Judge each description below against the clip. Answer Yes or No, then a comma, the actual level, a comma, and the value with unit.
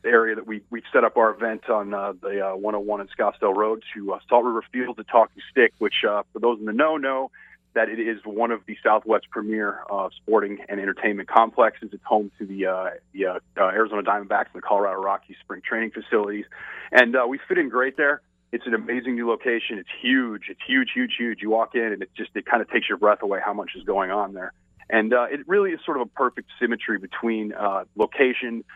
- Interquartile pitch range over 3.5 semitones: No, average, 2.9 semitones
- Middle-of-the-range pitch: No, low, 115 Hz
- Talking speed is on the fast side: Yes, fast, 230 wpm